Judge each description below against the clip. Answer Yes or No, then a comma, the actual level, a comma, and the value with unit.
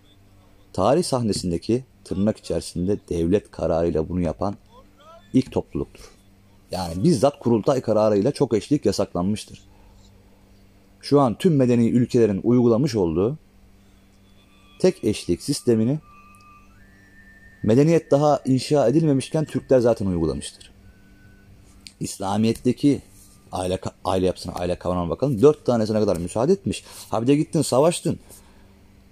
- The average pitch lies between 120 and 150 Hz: No, low, 100 Hz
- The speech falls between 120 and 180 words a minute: No, average, 105 wpm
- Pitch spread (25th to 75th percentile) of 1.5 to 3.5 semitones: No, average, 4.0 semitones